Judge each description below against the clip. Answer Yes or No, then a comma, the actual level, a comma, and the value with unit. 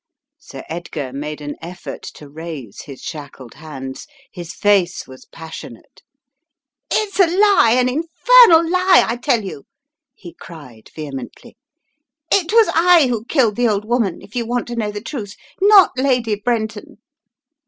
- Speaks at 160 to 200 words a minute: No, average, 150 wpm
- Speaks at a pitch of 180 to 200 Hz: No, high, 215 Hz